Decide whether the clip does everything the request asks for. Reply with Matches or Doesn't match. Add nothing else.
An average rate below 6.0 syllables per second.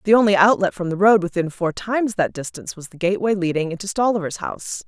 Doesn't match